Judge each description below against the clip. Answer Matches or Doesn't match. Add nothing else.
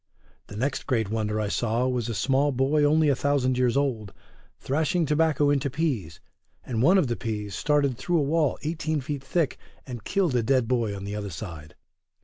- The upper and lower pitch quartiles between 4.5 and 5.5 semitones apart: Matches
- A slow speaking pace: Doesn't match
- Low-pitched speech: Matches